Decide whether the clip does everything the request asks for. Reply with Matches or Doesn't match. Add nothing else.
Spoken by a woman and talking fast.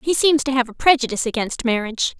Matches